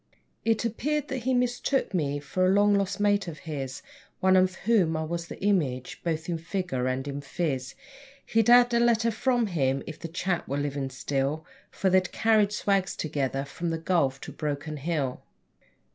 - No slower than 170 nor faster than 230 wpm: Yes, average, 190 wpm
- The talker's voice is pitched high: No, medium, 170 Hz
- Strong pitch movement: Yes, wide, 6.3 semitones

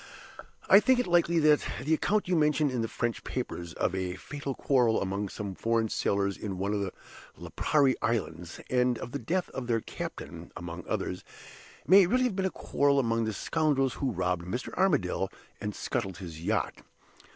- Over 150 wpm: Yes, average, 185 wpm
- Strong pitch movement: Yes, wide, 7.7 semitones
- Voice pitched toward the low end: Yes, low, 120 Hz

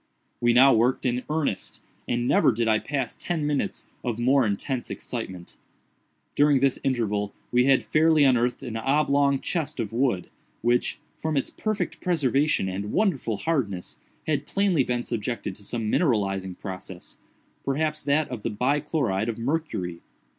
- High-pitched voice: No, low, 125 Hz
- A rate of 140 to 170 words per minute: Yes, average, 150 wpm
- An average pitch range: Yes, average, 4.9 semitones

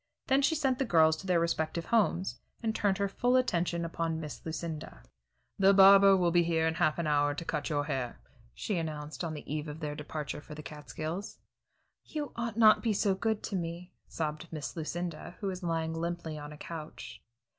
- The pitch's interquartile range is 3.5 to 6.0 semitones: Yes, average, 3.9 semitones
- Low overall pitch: No, medium, 170 Hz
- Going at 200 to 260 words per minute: Yes, fast, 205 wpm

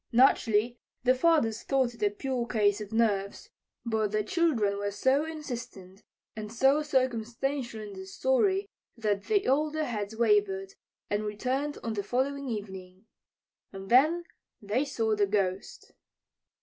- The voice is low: No, high, 230 Hz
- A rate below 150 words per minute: Yes, average, 140 wpm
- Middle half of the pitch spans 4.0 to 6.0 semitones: Yes, average, 4.6 semitones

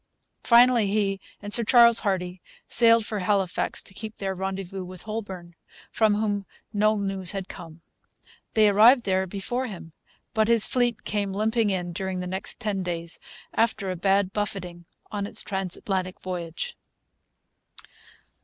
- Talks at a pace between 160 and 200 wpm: No, average, 145 wpm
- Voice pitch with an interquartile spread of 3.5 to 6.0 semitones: No, average, 2.7 semitones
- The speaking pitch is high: Yes, high, 195 Hz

